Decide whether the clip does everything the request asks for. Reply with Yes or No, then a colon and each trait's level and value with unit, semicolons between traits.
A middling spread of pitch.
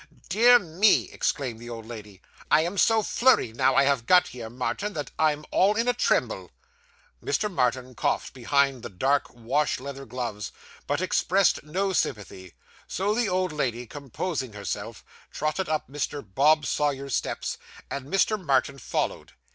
No: wide, 7.0 semitones